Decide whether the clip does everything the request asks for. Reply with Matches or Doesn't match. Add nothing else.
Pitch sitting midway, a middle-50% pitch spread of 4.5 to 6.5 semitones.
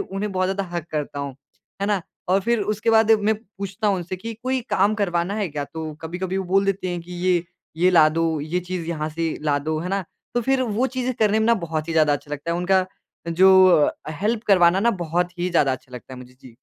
Doesn't match